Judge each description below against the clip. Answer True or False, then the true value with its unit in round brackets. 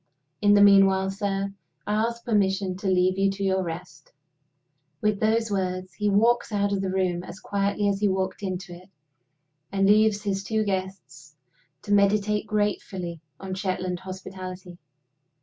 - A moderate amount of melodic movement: False (1.7 semitones)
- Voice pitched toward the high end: True (195 Hz)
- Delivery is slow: False (155 wpm)